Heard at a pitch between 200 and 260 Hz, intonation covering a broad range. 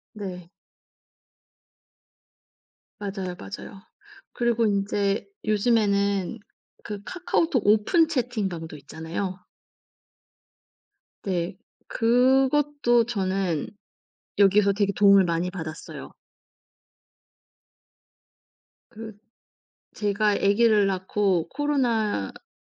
No: high, 205 Hz; average, 3.6 semitones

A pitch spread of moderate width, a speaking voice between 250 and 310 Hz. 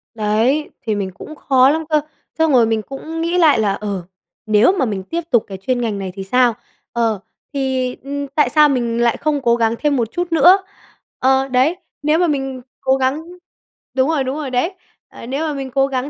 Yes: average, 4.5 semitones; very high, 265 Hz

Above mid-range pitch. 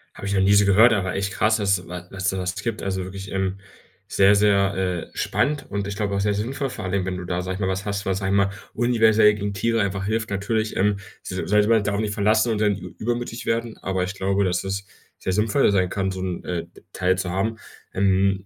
No: low, 100 Hz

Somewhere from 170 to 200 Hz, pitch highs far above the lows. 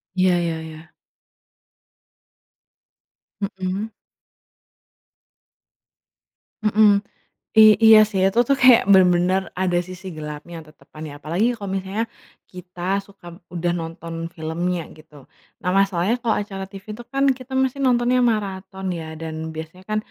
No: high, 190 Hz; average, 4.1 semitones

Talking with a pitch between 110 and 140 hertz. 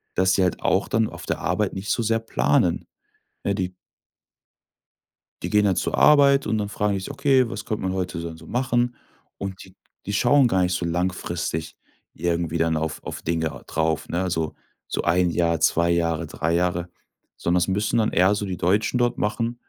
No: very low, 95 Hz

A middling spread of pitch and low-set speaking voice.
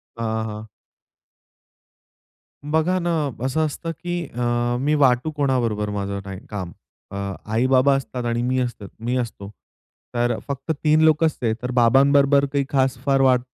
Yes: average, 3.4 semitones; low, 130 Hz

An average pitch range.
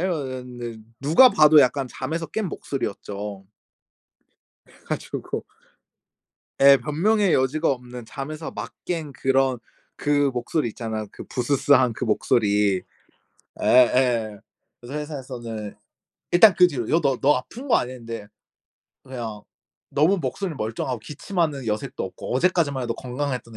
Yes: average, 4.3 semitones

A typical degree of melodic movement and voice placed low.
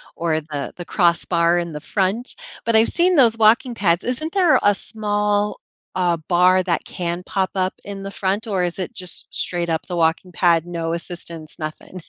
No: average, 3.5 semitones; medium, 185 Hz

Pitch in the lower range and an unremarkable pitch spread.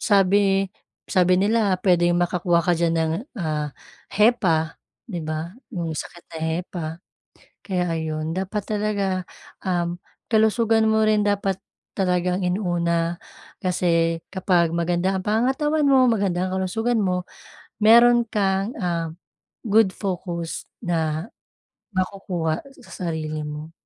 No: medium, 185 Hz; average, 3.2 semitones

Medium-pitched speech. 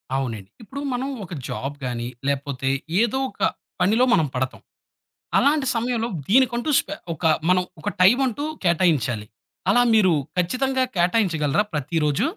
Yes: medium, 180 Hz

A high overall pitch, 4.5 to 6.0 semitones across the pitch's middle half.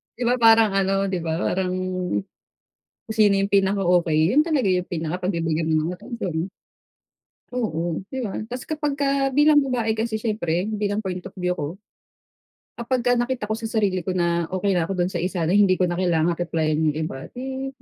Yes: high, 195 Hz; average, 4.9 semitones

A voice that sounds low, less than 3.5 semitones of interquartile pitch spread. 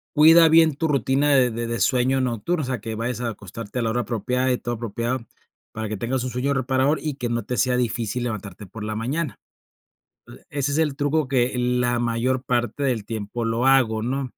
Yes: low, 125 Hz; average, 2.7 semitones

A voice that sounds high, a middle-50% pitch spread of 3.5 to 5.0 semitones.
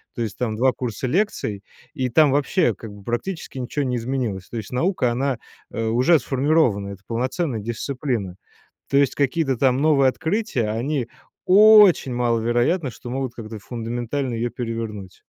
No: low, 125 Hz; average, 3.8 semitones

